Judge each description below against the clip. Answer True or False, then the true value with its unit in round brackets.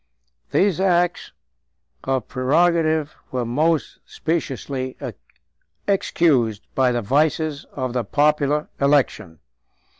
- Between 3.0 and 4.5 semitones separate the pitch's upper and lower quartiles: True (3.8 semitones)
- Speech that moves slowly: True (90 wpm)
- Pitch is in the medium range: True (145 Hz)